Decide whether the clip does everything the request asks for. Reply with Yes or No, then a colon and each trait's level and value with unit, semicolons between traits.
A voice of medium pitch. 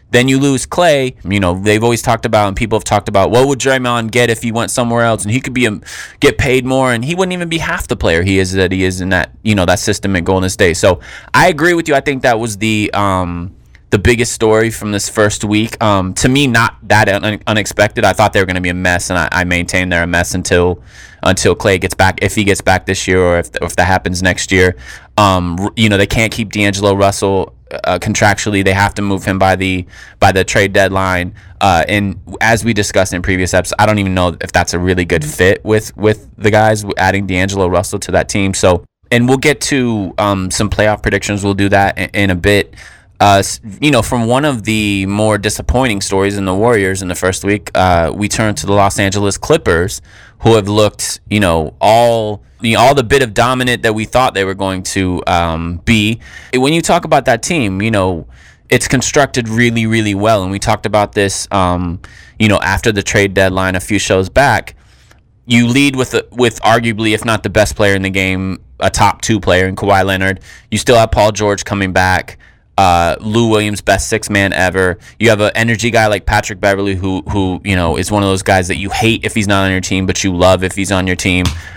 No: low, 100 Hz